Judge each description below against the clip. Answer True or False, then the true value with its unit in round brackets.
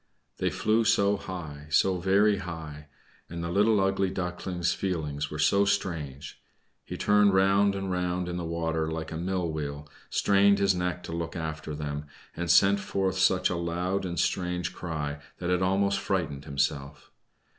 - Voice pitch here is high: False (90 Hz)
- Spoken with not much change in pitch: False (3.5 semitones)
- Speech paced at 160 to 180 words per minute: True (165 wpm)